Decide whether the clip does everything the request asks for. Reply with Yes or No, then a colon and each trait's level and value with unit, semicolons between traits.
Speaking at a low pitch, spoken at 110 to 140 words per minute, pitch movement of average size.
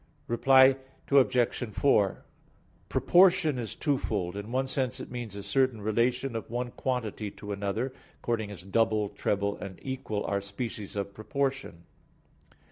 Yes: low, 115 Hz; slow, 135 wpm; average, 4.4 semitones